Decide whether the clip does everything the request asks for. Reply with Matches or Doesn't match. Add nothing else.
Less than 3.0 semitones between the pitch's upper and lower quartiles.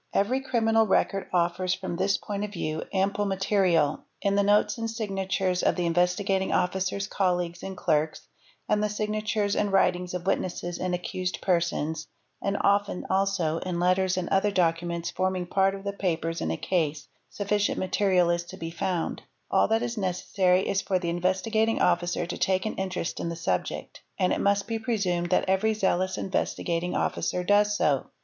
Matches